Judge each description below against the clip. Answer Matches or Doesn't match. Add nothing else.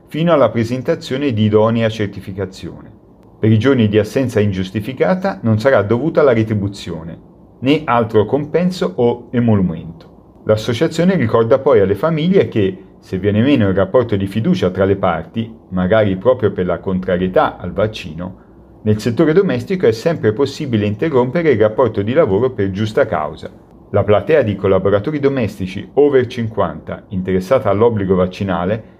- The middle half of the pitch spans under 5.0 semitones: Doesn't match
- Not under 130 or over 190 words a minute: Matches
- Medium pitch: Doesn't match